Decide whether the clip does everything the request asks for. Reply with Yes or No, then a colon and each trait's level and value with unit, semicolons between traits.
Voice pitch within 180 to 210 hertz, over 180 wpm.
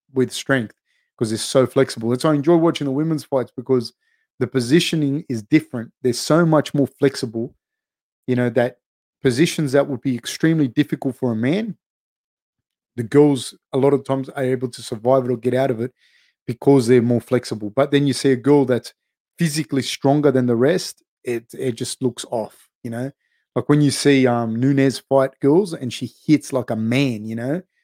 No: low, 135 Hz; average, 195 wpm